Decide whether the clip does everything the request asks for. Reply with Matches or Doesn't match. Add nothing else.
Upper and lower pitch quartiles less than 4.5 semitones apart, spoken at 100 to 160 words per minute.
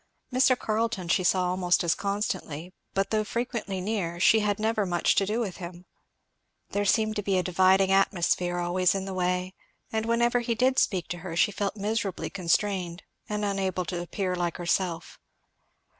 Doesn't match